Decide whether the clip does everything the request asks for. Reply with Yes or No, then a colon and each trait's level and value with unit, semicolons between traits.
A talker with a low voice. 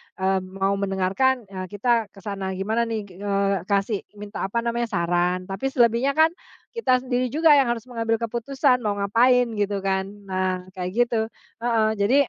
No: high, 215 Hz